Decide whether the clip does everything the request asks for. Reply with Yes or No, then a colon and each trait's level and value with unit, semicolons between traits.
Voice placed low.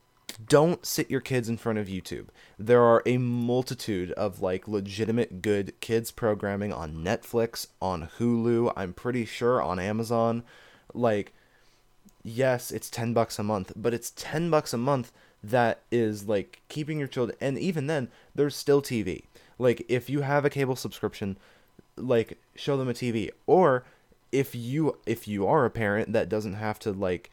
Yes: low, 115 Hz